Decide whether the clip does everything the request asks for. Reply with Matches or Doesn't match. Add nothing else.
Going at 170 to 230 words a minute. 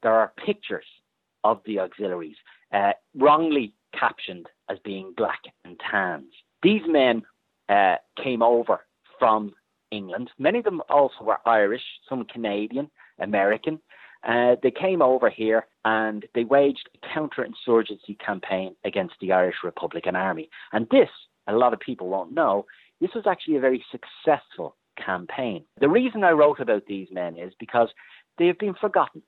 Doesn't match